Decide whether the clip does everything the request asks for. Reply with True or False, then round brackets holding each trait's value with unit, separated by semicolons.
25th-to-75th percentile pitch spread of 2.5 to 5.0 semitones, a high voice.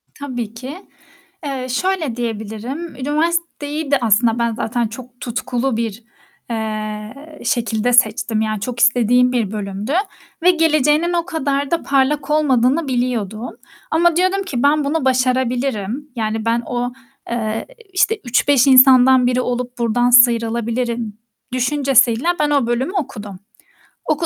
True (3.8 semitones; 250 Hz)